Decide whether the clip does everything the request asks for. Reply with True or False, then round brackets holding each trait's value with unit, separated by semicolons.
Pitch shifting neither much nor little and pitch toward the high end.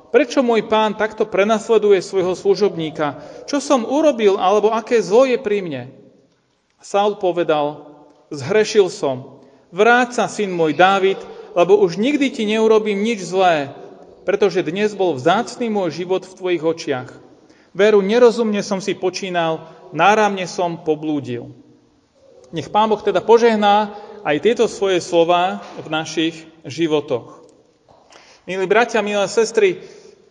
True (4.6 semitones; 200 Hz)